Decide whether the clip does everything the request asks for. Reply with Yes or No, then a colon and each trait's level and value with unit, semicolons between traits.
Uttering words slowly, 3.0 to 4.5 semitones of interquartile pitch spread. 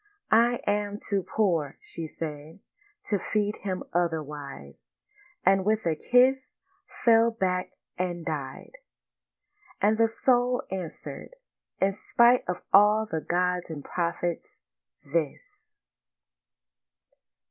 No: slow, 105 wpm; average, 5.1 semitones